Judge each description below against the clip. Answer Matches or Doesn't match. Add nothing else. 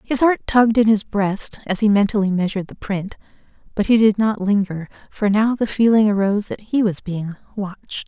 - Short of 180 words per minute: Doesn't match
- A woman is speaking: Matches